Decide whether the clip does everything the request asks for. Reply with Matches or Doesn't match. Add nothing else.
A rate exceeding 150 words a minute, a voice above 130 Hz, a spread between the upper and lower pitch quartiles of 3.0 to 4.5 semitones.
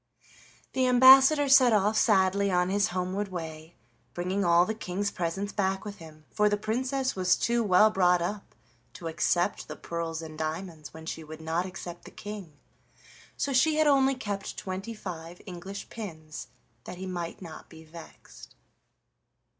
Matches